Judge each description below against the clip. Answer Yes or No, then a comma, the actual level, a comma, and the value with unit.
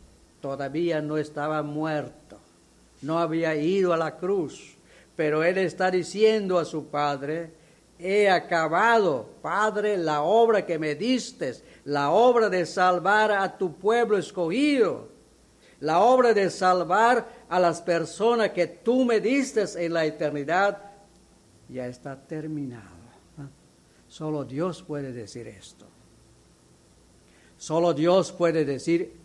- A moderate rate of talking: No, slow, 120 wpm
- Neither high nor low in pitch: Yes, medium, 170 Hz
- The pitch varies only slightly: No, average, 5.3 semitones